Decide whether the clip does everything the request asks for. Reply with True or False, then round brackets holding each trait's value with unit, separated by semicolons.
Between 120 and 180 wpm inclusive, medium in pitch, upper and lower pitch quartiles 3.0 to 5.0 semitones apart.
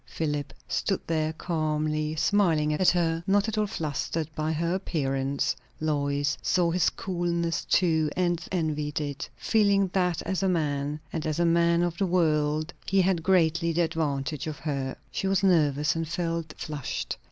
False (165 wpm; 165 Hz; 2.6 semitones)